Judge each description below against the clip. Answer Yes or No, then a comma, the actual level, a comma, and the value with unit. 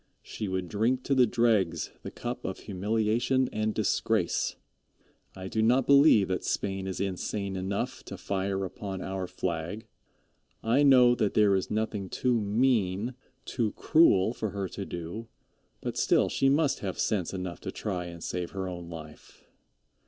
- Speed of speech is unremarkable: Yes, average, 160 wpm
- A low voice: Yes, low, 100 Hz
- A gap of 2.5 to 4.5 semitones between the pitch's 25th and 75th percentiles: Yes, average, 3.8 semitones